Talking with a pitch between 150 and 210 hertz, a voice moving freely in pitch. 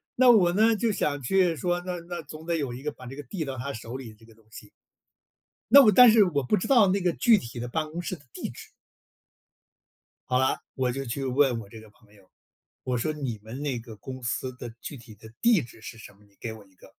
No: low, 135 Hz; wide, 7.0 semitones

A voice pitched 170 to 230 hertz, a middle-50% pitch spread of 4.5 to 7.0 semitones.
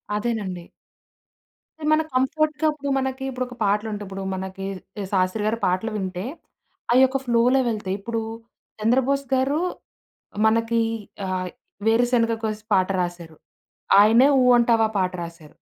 Yes: high, 225 Hz; average, 5.0 semitones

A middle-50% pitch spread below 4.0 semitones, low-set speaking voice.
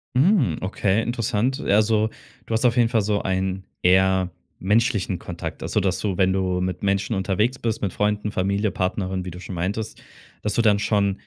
Yes: average, 2.8 semitones; low, 100 Hz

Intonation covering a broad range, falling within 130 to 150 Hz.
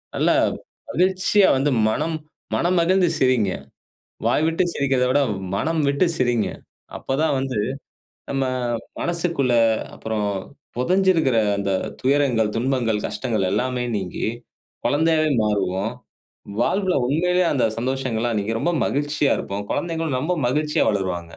Yes: wide, 6.2 semitones; low, 135 Hz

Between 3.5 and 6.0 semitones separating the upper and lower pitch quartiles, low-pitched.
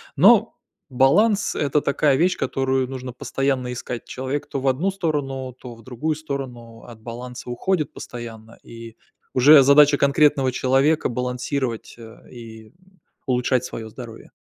No: average, 2.7 semitones; low, 130 Hz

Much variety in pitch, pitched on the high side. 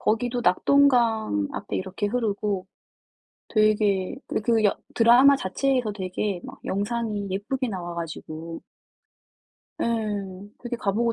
No: average, 3.7 semitones; high, 210 Hz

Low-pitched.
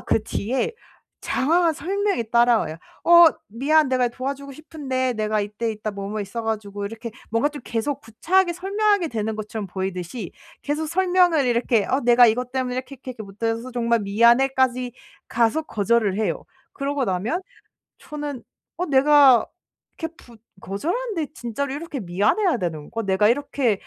No: high, 245 Hz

